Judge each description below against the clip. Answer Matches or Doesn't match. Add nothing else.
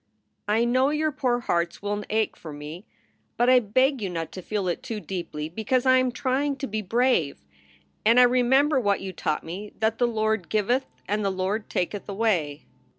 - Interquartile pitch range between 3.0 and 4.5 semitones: Doesn't match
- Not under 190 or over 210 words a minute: Matches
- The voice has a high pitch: Matches